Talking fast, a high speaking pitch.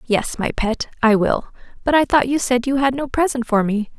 Yes: fast, 240 wpm; very high, 250 Hz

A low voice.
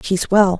No: high, 190 Hz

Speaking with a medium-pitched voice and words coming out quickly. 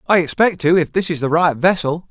Yes: medium, 170 Hz; fast, 255 wpm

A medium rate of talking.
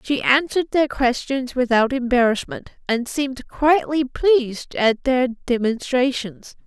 No: slow, 115 wpm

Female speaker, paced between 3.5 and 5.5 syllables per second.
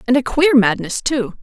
Yes: female; 4.7 syllables/s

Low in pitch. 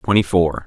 Yes: very low, 90 Hz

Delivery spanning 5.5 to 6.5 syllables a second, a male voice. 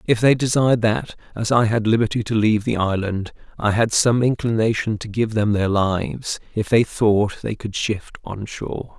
No: 4.9 syllables/s; male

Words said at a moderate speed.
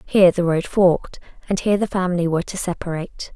Yes: average, 195 wpm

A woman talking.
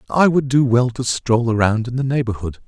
No: male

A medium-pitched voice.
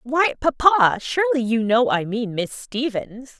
No: high, 240 Hz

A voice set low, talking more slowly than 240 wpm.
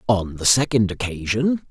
Yes: low, 115 Hz; average, 140 wpm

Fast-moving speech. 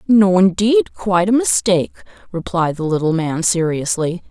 No: average, 140 wpm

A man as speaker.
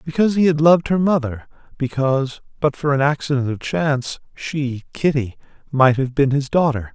Yes: male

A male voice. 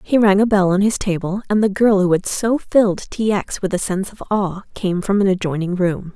No: female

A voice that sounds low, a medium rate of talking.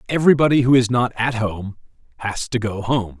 Yes: low, 115 Hz; average, 190 wpm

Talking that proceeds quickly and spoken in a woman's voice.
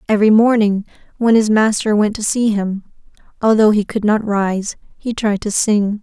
No: average, 180 wpm; female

